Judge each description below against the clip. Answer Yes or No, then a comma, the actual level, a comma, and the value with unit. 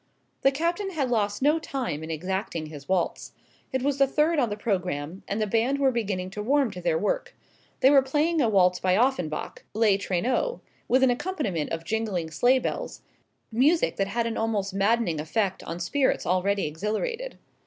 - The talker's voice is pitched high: Yes, high, 220 Hz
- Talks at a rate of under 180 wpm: No, average, 185 wpm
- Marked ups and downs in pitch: Yes, wide, 6.5 semitones